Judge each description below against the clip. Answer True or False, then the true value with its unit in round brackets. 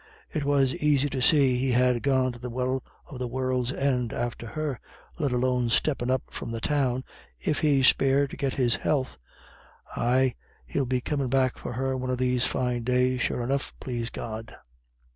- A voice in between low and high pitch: False (130 Hz)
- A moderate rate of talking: True (185 wpm)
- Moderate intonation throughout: False (1.7 semitones)